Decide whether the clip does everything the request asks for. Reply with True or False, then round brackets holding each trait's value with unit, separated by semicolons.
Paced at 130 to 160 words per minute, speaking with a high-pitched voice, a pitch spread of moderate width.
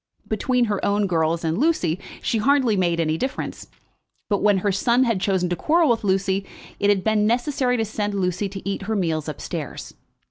False (200 wpm; 200 Hz; 4.0 semitones)